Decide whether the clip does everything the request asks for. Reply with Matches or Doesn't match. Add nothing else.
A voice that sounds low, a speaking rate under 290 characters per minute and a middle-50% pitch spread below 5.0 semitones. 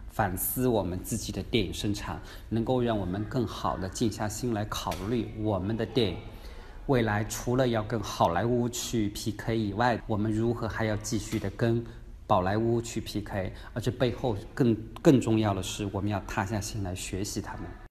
Matches